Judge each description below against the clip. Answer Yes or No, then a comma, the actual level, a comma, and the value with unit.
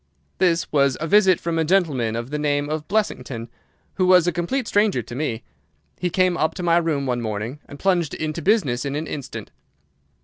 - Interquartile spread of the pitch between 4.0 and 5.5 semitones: Yes, average, 4.6 semitones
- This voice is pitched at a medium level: Yes, medium, 155 Hz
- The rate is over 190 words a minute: Yes, average, 200 wpm